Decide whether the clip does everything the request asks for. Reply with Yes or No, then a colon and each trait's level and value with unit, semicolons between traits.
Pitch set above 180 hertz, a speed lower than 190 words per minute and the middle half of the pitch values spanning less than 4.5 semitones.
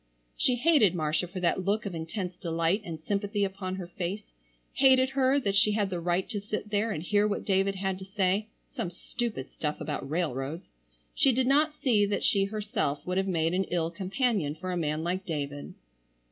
No: high, 190 Hz; average, 195 wpm; average, 3.7 semitones